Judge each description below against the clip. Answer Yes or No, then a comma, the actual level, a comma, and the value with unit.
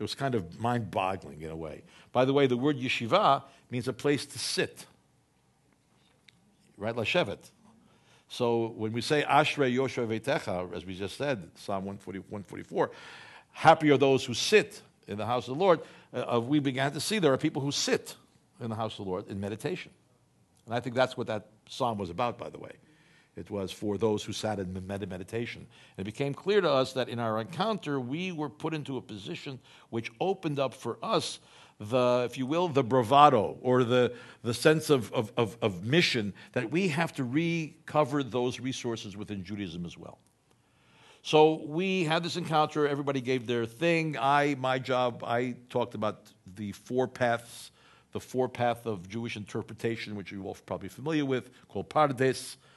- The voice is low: Yes, low, 125 Hz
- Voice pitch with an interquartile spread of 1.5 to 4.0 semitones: No, average, 4.9 semitones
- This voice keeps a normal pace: Yes, average, 180 wpm